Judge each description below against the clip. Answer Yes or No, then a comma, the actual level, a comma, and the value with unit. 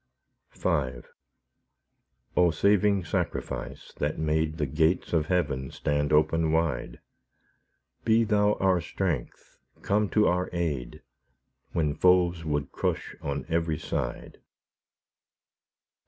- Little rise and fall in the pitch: No, average, 3.5 semitones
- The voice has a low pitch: Yes, very low, 80 Hz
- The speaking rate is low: Yes, slow, 105 wpm